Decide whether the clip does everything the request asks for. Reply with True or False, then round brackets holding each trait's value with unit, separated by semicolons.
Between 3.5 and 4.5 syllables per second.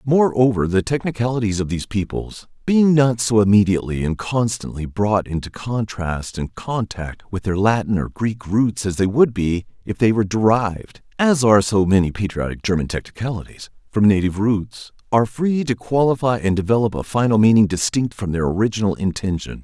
False (4.7 syllables/s)